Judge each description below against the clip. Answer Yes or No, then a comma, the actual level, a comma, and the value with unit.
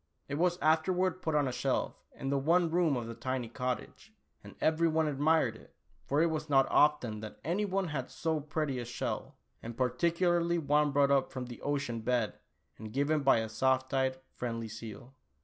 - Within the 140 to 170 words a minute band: No, average, 195 wpm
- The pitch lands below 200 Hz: Yes, medium, 140 Hz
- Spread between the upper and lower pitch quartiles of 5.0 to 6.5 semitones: No, average, 4.3 semitones